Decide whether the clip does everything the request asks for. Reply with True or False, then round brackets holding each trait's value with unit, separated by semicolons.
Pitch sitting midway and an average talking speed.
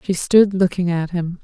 False (180 Hz; 210 wpm)